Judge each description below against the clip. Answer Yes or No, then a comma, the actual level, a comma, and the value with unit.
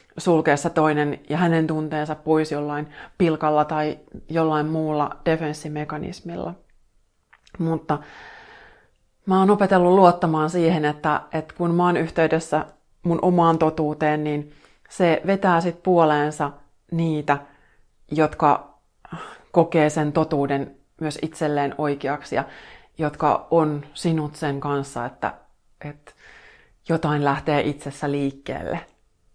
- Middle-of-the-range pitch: Yes, medium, 155 Hz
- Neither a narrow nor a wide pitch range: No, narrow, 2.0 semitones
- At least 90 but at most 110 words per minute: Yes, average, 105 wpm